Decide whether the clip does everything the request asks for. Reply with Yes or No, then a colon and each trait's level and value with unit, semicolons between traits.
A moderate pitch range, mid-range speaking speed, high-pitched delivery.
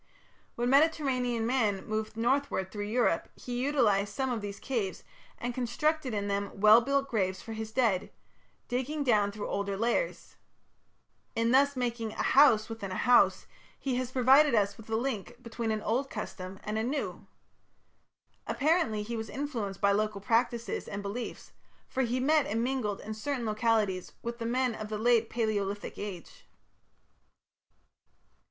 Yes: average, 3.5 semitones; average, 160 wpm; high, 230 Hz